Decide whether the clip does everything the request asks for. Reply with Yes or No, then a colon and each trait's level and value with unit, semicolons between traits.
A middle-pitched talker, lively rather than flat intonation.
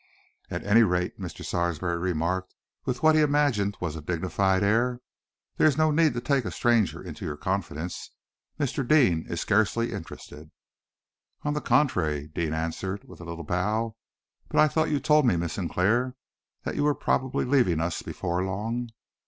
No: low, 100 Hz; wide, 7.0 semitones